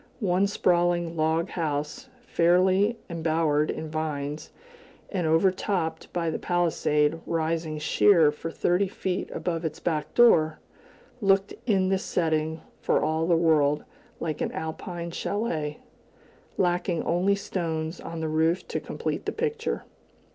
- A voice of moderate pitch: Yes, medium, 165 Hz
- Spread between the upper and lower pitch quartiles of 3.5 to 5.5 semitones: No, average, 2.7 semitones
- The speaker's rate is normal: No, slow, 130 wpm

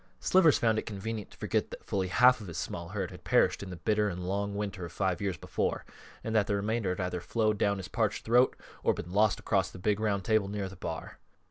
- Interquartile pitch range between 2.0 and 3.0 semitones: Yes, narrow, 2.6 semitones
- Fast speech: Yes, fast, 245 wpm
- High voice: No, low, 100 Hz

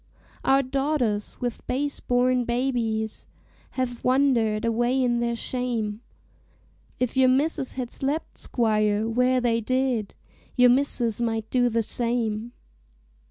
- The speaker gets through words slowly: Yes, slow, 120 wpm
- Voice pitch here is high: Yes, high, 245 Hz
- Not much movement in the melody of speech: Yes, narrow, 2.2 semitones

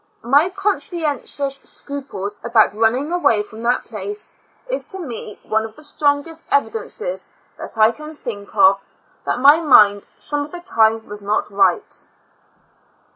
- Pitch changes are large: Yes, wide, 6.3 semitones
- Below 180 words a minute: Yes, average, 145 wpm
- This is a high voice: Yes, very high, 275 Hz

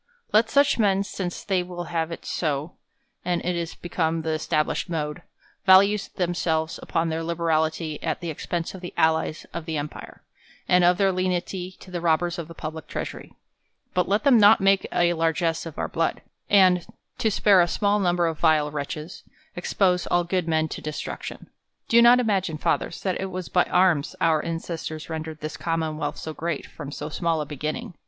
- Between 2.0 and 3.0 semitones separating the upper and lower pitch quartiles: Yes, narrow, 2.5 semitones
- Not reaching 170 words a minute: No, average, 190 wpm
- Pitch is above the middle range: No, medium, 170 Hz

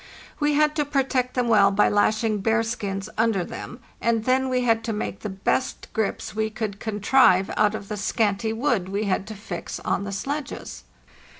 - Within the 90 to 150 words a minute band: No, average, 185 wpm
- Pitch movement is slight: No, average, 3.7 semitones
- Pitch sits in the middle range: No, high, 220 Hz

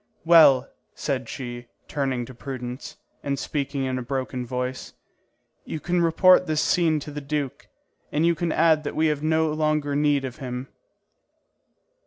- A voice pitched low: No, medium, 145 Hz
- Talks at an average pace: Yes, average, 160 wpm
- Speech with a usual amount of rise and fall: Yes, average, 3.2 semitones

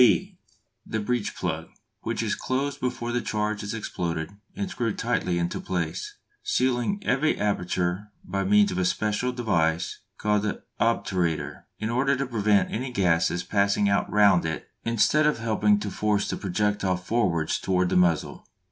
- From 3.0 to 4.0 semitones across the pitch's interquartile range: No, average, 4.6 semitones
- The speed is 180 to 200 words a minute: No, average, 160 wpm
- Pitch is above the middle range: No, low, 105 Hz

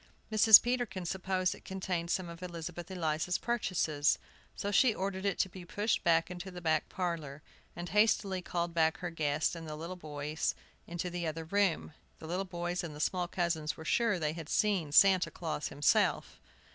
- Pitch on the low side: No, medium, 175 Hz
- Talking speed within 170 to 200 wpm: Yes, average, 180 wpm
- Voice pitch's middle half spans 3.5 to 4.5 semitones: No, average, 2.9 semitones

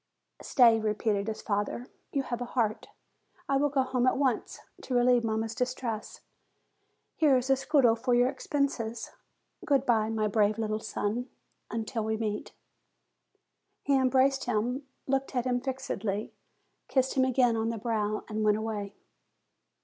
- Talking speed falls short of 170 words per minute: Yes, average, 150 wpm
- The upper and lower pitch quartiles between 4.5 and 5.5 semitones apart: No, average, 3.2 semitones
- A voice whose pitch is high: Yes, high, 240 Hz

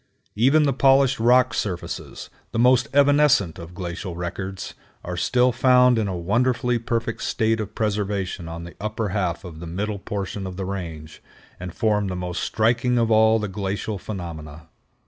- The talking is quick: No, average, 165 wpm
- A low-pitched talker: Yes, low, 105 Hz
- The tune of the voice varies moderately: Yes, average, 4.8 semitones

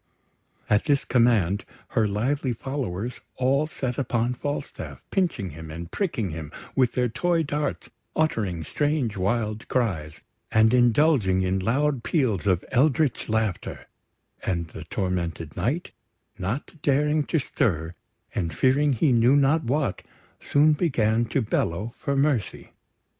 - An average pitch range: No, wide, 6.6 semitones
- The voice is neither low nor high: No, low, 120 Hz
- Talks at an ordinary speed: No, slow, 130 wpm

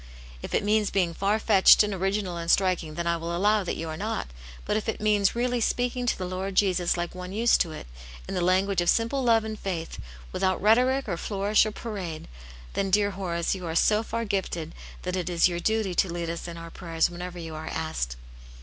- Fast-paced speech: Yes, fast, 230 wpm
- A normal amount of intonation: Yes, average, 3.7 semitones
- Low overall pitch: No, high, 190 Hz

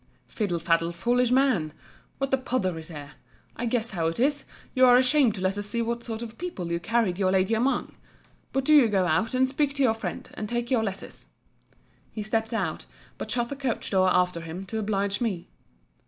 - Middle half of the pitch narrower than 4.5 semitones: No, average, 5.1 semitones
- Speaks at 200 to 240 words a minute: Yes, fast, 205 wpm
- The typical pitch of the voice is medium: No, high, 225 Hz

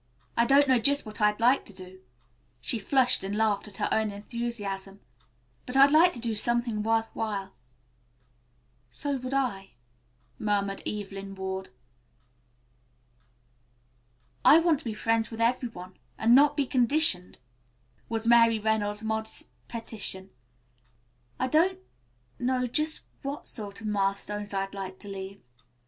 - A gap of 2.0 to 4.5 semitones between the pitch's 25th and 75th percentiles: Yes, average, 4.0 semitones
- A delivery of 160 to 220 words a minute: No, average, 140 wpm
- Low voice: No, high, 220 Hz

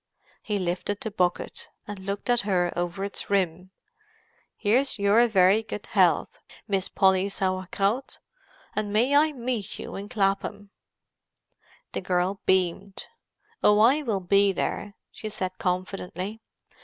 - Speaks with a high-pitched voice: Yes, high, 200 Hz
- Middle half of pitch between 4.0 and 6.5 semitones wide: No, narrow, 2.4 semitones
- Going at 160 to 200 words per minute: No, slow, 135 wpm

